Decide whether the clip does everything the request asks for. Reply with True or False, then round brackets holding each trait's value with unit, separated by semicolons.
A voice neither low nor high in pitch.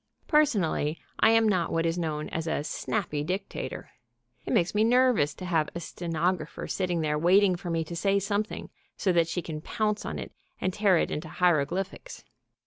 True (175 Hz)